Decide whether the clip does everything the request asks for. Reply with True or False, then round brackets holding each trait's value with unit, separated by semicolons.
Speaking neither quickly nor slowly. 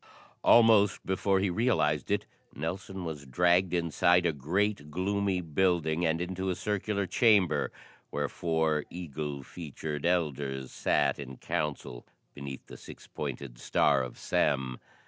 False (130 wpm)